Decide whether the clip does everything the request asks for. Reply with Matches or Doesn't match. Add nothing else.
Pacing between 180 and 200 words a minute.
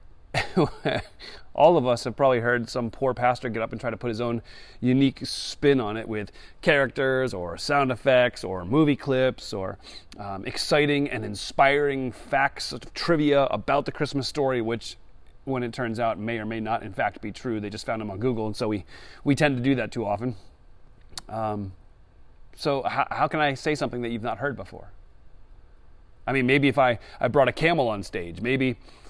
Matches